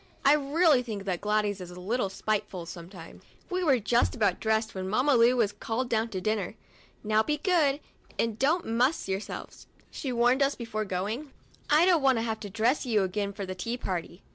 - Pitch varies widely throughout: No, average, 4.9 semitones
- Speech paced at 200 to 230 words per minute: Yes, fast, 205 wpm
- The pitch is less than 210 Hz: No, high, 225 Hz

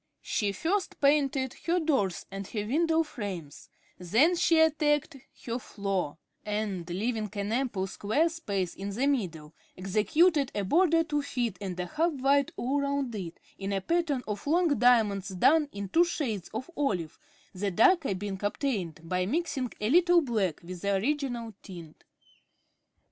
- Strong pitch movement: Yes, wide, 7.2 semitones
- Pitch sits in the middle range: No, high, 230 Hz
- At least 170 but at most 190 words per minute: No, average, 155 wpm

